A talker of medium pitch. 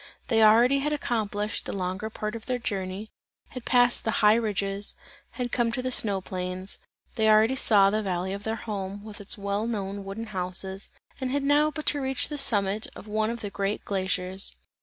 No: high, 215 Hz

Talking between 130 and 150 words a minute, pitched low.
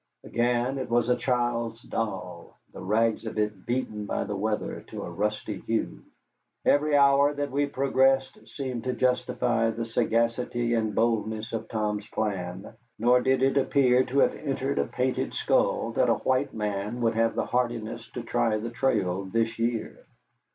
No: average, 165 wpm; low, 115 Hz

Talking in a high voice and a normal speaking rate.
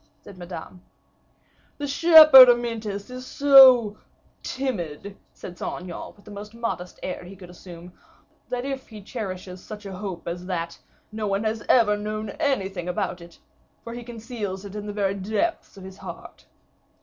Yes: high, 205 Hz; average, 165 wpm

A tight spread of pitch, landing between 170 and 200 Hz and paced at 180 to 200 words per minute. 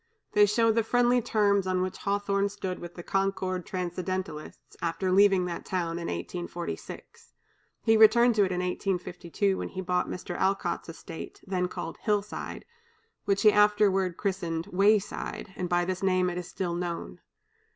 No: narrow, 2.3 semitones; medium, 185 Hz; average, 160 wpm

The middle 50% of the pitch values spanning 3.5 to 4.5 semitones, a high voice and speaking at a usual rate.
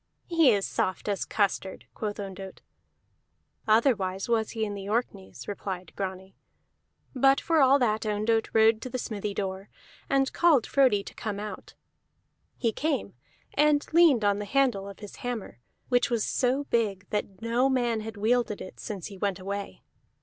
Yes: average, 3.8 semitones; high, 215 Hz; average, 165 wpm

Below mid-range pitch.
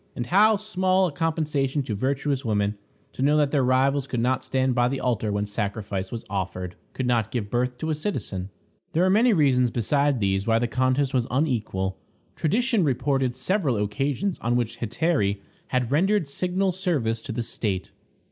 Yes: low, 130 Hz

